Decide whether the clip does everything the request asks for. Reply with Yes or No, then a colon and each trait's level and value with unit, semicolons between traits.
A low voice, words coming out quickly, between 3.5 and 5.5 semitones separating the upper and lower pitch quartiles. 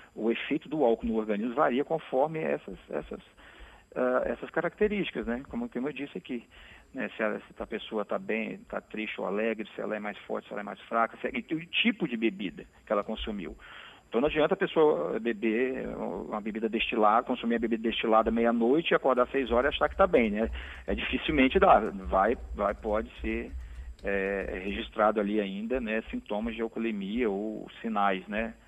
No: low, 115 Hz; fast, 195 wpm; average, 2.8 semitones